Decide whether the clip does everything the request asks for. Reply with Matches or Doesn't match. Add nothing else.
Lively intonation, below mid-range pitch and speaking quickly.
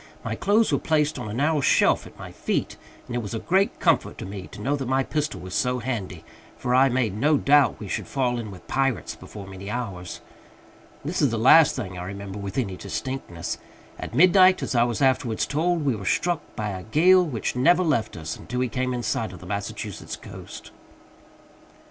Matches